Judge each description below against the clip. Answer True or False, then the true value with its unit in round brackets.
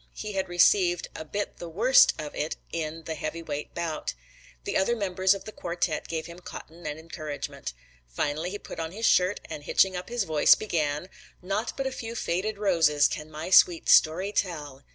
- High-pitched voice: False (170 Hz)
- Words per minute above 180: True (190 wpm)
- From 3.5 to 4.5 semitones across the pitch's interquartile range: True (3.9 semitones)